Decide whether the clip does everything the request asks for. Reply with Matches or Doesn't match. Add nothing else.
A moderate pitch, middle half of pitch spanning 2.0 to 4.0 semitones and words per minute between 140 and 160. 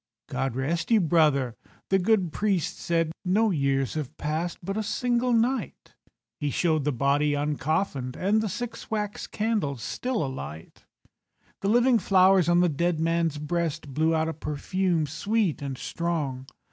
Doesn't match